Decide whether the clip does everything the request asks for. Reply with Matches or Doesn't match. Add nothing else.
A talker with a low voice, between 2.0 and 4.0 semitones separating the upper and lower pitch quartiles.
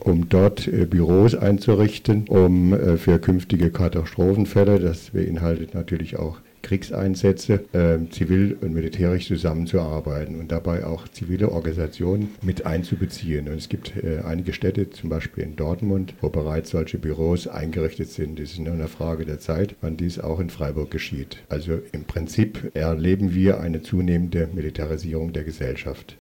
Matches